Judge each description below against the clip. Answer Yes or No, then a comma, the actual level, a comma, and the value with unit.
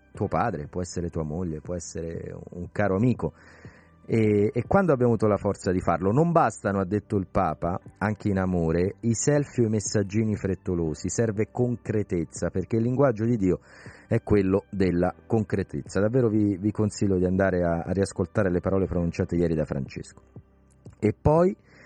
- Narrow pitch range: No, average, 3.9 semitones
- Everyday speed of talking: No, fast, 175 wpm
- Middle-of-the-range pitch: No, low, 100 Hz